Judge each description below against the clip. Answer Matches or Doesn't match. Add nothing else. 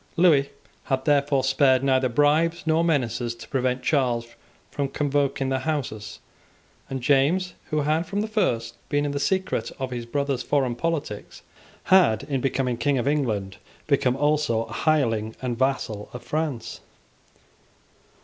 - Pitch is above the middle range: Doesn't match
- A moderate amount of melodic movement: Matches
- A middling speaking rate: Matches